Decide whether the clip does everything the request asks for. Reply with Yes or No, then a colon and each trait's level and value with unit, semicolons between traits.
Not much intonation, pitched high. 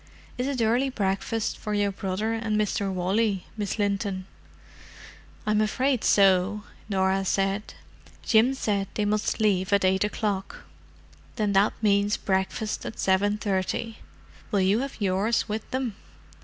Yes: narrow, 2.1 semitones; high, 205 Hz